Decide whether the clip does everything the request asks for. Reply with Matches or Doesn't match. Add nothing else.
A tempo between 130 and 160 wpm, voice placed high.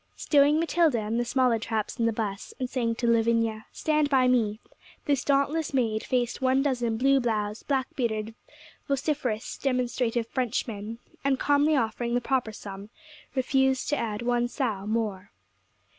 Matches